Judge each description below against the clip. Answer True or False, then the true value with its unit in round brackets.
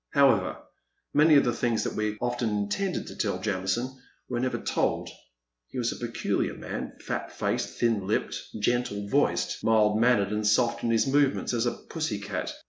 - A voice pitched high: False (115 Hz)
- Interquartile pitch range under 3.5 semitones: True (3.0 semitones)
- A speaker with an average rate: True (175 wpm)